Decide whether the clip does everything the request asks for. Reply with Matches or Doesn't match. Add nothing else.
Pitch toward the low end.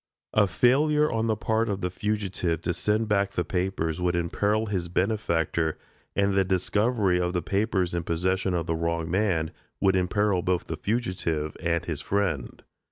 Matches